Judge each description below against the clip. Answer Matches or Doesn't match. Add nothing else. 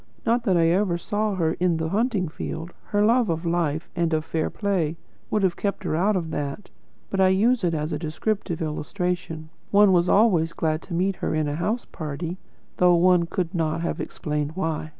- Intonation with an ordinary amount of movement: Matches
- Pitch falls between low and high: Matches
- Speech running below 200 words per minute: Doesn't match